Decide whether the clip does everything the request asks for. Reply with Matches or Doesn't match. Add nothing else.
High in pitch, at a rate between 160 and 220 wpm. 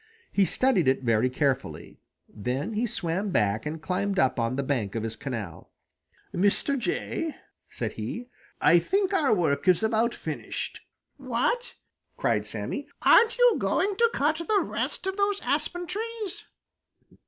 Doesn't match